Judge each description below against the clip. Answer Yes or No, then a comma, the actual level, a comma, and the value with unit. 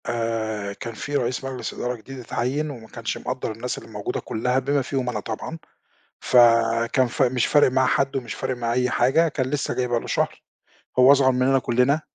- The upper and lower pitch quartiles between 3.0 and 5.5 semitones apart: No, narrow, 2.4 semitones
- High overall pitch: No, low, 125 Hz